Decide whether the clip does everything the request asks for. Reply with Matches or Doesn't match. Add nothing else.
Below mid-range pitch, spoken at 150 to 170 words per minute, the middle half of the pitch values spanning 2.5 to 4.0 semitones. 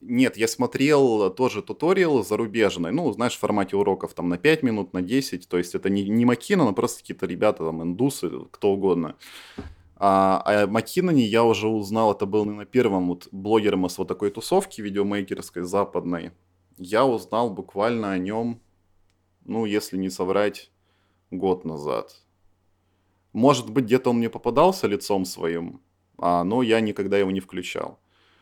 Matches